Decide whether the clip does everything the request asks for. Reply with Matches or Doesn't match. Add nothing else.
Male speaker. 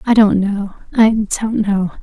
Doesn't match